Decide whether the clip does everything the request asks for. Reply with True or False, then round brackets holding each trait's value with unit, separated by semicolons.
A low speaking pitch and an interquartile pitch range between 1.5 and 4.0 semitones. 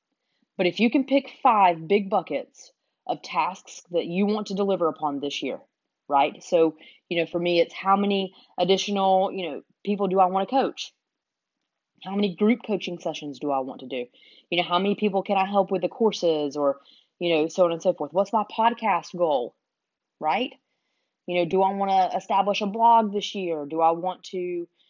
False (190 Hz; 2.9 semitones)